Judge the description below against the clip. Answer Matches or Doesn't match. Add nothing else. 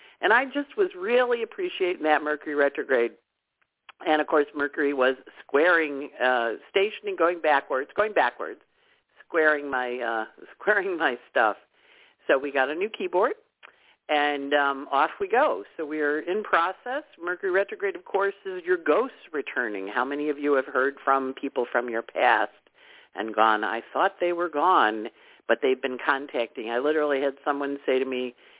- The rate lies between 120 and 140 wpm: Doesn't match